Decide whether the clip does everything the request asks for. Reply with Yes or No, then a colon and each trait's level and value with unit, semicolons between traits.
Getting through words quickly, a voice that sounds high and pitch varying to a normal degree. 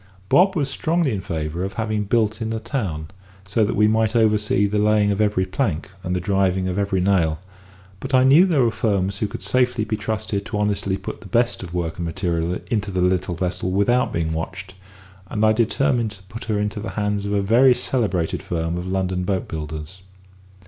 No: fast, 210 wpm; low, 100 Hz; average, 3.3 semitones